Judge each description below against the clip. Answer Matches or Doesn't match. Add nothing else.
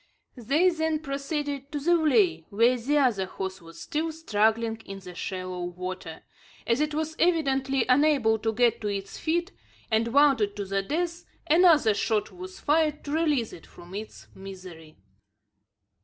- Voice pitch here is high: Matches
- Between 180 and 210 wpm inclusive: Doesn't match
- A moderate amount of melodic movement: Doesn't match